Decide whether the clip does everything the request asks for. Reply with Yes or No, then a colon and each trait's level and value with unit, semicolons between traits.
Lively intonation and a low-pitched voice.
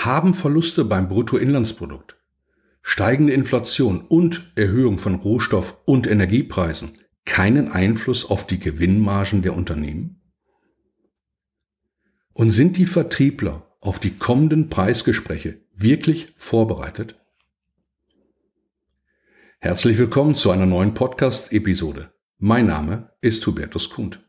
Yes: wide, 6.4 semitones; low, 110 Hz